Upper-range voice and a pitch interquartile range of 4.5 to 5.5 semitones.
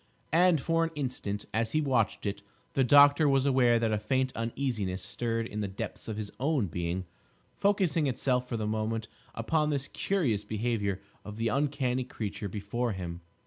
No: low, 120 Hz; average, 4.8 semitones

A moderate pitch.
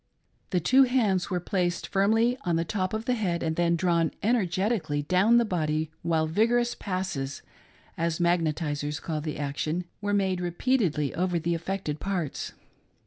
Yes: medium, 175 Hz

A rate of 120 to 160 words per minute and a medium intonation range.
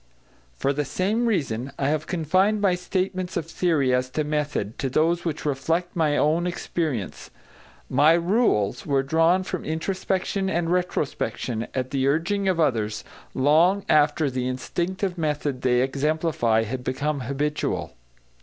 Yes: average, 145 wpm; average, 4.9 semitones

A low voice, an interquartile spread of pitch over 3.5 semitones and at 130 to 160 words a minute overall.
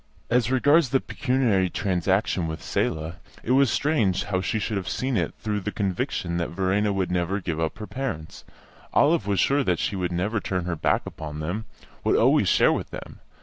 No: very low, 95 Hz; average, 4.7 semitones; average, 195 wpm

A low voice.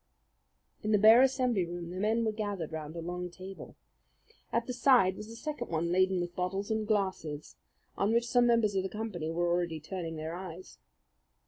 No: high, 190 Hz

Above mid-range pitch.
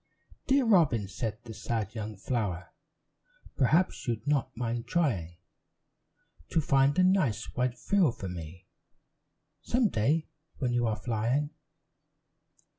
No: low, 120 Hz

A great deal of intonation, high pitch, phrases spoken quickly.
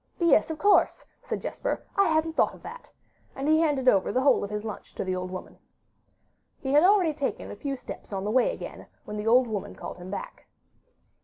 Yes: wide, 7.2 semitones; very high, 265 Hz; fast, 220 wpm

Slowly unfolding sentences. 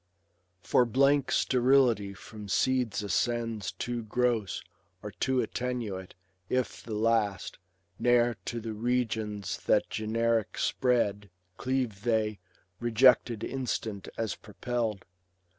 Yes: slow, 105 wpm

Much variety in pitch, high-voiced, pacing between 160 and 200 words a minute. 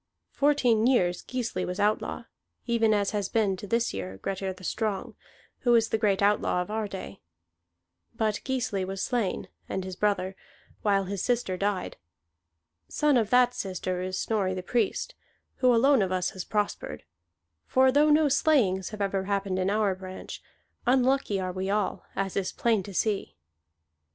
No: average, 3.8 semitones; high, 205 Hz; average, 165 wpm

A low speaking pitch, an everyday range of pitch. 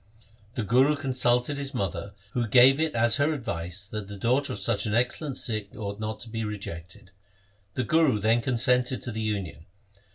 Yes: low, 115 Hz; average, 4.0 semitones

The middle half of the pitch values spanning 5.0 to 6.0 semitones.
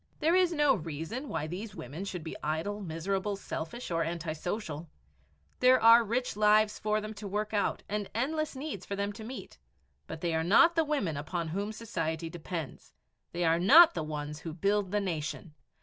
Yes: average, 5.3 semitones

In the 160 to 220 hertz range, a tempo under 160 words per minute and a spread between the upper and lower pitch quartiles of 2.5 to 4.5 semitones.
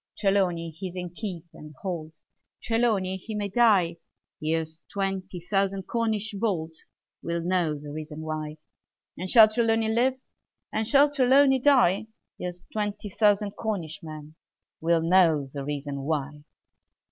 No: medium, 185 Hz; slow, 135 wpm; average, 5.2 semitones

